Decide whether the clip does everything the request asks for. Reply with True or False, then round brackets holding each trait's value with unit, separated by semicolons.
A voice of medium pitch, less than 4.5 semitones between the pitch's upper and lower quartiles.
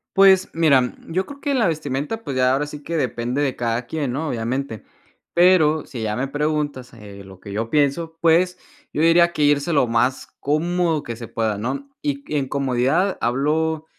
False (145 Hz; 5.0 semitones)